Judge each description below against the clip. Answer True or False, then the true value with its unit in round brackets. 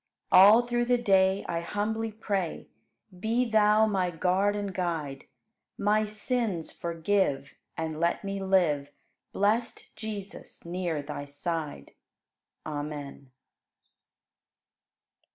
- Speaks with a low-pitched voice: False (190 Hz)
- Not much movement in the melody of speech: False (4.6 semitones)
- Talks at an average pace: False (100 wpm)